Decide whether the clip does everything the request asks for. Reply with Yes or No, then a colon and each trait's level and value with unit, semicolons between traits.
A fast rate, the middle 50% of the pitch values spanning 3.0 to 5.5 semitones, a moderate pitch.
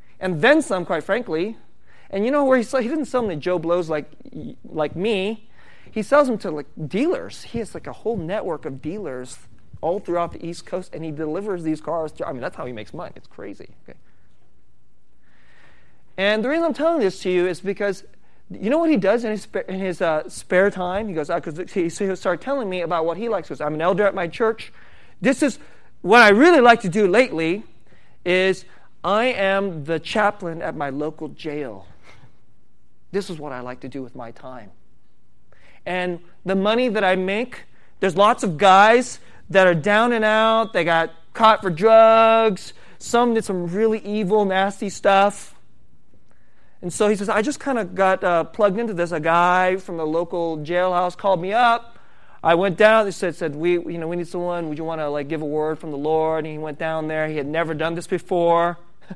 Yes: fast, 215 wpm; average, 4.8 semitones; medium, 180 Hz